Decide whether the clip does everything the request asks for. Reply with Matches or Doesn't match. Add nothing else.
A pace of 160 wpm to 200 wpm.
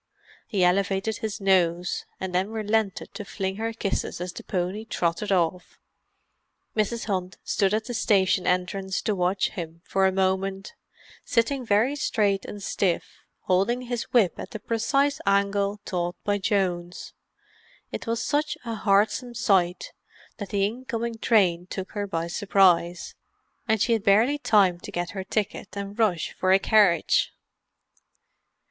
Doesn't match